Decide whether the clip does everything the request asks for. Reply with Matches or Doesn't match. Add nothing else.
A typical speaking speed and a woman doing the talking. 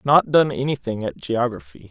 Doesn't match